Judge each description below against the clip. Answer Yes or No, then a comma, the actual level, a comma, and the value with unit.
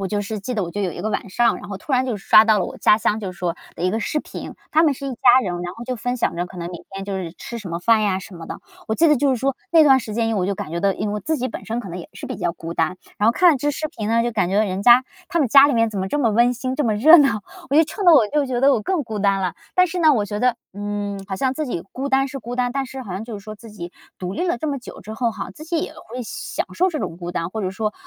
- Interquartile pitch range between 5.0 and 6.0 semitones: Yes, average, 5.3 semitones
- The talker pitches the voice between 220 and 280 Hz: Yes, high, 225 Hz